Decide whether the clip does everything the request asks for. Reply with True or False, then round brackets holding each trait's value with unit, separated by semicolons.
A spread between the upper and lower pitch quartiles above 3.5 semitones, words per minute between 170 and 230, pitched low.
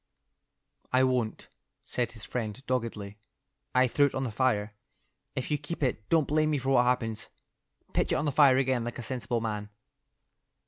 False (3.0 semitones; 180 wpm; 125 Hz)